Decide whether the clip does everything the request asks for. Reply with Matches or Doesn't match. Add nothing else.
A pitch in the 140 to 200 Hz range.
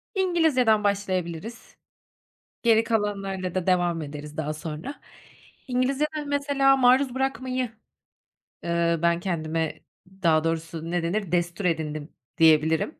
Matches